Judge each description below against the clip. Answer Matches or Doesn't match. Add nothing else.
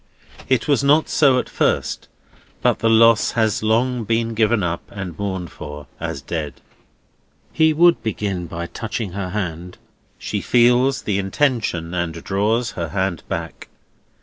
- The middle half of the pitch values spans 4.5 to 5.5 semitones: Matches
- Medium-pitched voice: Doesn't match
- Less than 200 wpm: Matches